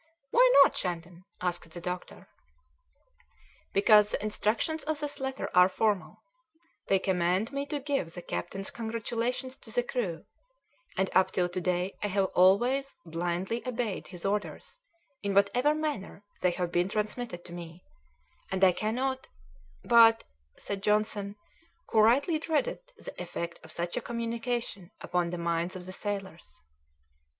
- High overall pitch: Yes, high, 200 Hz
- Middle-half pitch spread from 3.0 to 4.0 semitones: No, average, 5.1 semitones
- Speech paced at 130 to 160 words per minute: Yes, average, 150 wpm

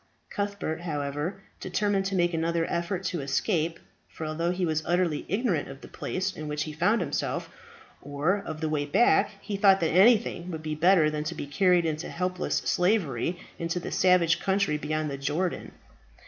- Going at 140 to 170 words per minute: No, average, 180 wpm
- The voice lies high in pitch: No, medium, 170 Hz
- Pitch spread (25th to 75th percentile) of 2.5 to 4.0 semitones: Yes, average, 3.4 semitones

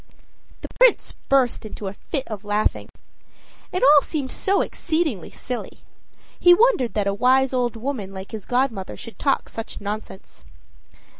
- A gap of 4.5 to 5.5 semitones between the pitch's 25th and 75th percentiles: Yes, average, 5.1 semitones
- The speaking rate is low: No, average, 150 wpm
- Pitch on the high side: Yes, very high, 250 Hz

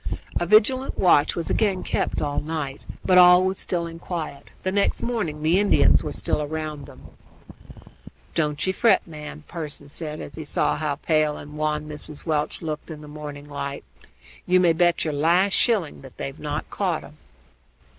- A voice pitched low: No, medium, 155 Hz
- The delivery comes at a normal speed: Yes, average, 185 wpm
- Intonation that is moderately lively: Yes, average, 3.1 semitones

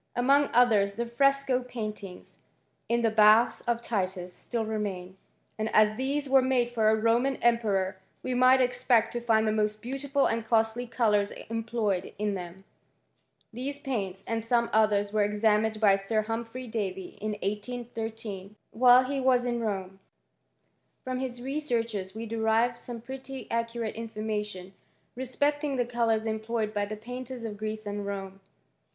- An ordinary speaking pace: Yes, average, 145 wpm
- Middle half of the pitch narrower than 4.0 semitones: Yes, average, 2.7 semitones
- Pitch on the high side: Yes, high, 225 Hz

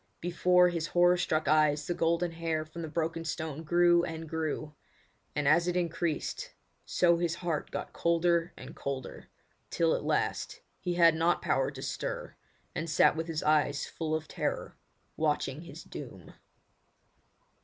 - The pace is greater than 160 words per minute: No, average, 155 wpm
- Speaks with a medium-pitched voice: Yes, medium, 165 Hz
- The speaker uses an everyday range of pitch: No, narrow, 1.8 semitones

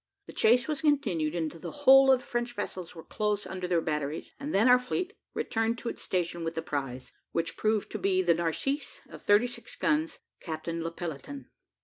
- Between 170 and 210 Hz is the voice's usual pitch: Yes, high, 190 Hz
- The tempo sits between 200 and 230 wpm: Yes, fast, 205 wpm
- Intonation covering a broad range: Yes, wide, 7.2 semitones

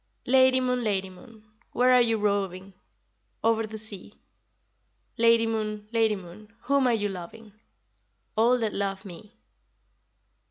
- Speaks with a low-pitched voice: No, high, 220 Hz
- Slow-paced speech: Yes, slow, 130 wpm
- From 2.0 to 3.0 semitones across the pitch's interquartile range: Yes, narrow, 2.5 semitones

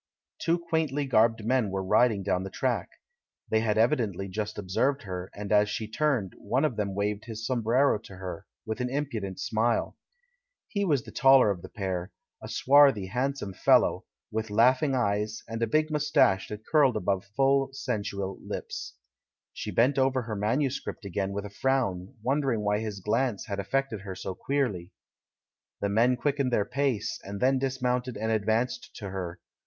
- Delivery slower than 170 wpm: No, average, 175 wpm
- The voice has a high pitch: No, low, 110 Hz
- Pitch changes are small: No, average, 4.7 semitones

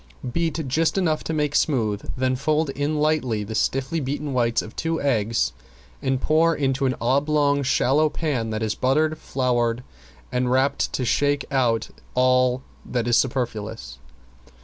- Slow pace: No, average, 150 wpm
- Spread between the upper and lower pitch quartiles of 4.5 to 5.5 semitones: No, average, 3.7 semitones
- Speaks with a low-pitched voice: Yes, low, 130 Hz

